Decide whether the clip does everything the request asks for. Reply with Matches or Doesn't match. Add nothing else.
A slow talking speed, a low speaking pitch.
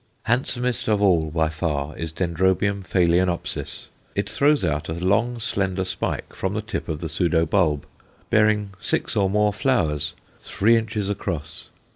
Doesn't match